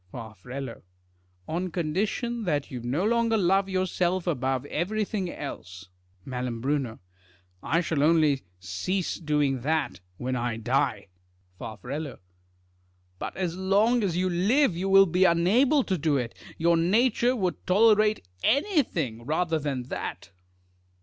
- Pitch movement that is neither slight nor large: No, wide, 7.4 semitones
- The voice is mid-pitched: Yes, medium, 165 Hz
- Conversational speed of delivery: No, slow, 125 wpm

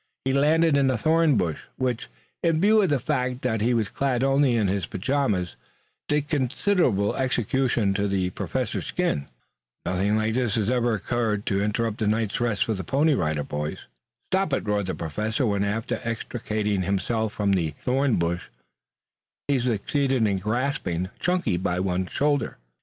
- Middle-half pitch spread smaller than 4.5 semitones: No, average, 5.3 semitones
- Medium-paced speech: Yes, average, 170 wpm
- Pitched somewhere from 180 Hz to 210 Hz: No, low, 115 Hz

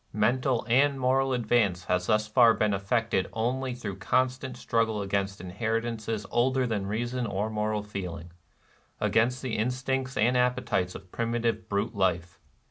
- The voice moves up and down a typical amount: Yes, average, 3.7 semitones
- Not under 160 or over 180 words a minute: No, average, 150 wpm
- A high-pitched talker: No, low, 115 Hz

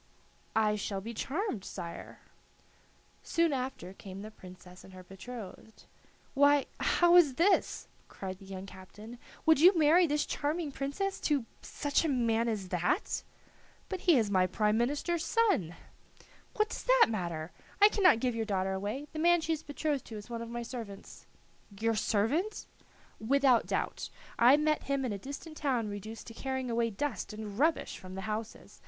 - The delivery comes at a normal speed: Yes, average, 170 wpm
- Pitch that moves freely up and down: Yes, wide, 6.6 semitones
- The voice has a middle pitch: No, high, 235 Hz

